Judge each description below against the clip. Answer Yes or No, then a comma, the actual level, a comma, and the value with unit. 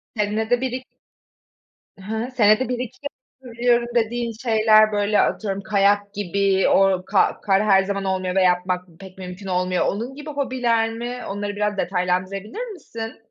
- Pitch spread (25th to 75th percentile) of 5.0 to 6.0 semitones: No, average, 3.5 semitones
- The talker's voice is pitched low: No, high, 210 Hz